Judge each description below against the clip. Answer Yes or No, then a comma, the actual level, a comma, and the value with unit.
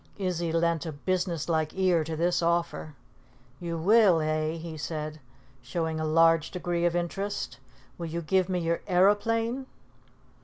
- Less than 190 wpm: Yes, average, 150 wpm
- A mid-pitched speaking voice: Yes, medium, 170 Hz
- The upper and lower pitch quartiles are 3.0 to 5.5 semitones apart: No, narrow, 2.4 semitones